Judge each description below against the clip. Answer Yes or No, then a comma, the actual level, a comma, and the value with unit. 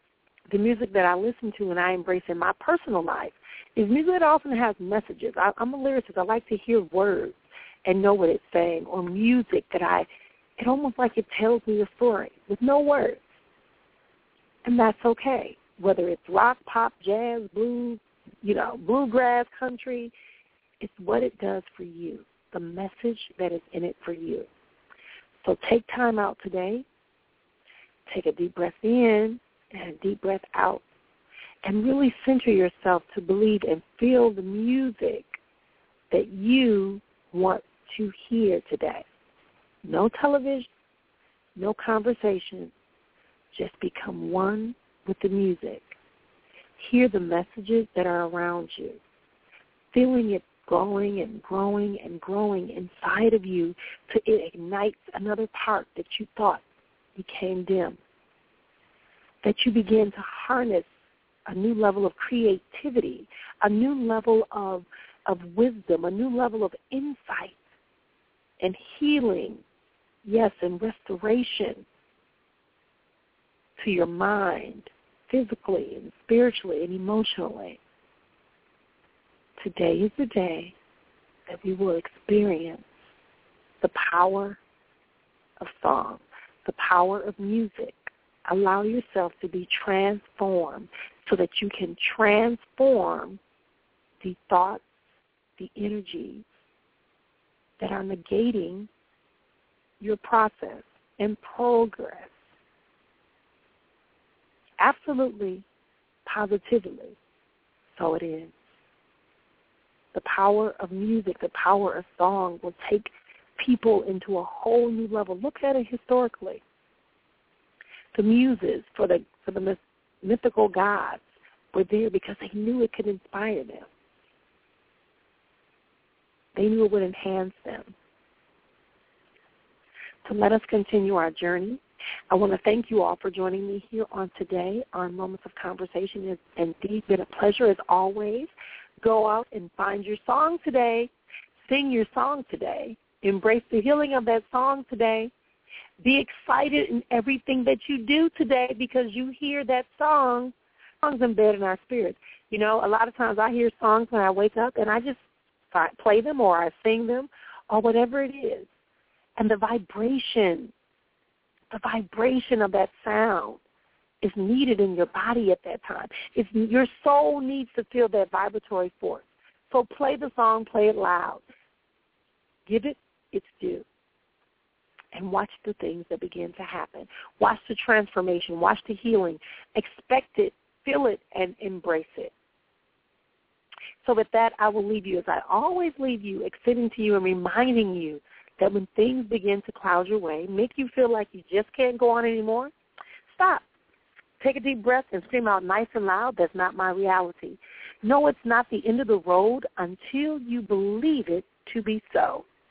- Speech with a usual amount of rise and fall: Yes, average, 4.2 semitones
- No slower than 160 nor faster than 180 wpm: No, average, 140 wpm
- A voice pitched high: Yes, high, 215 Hz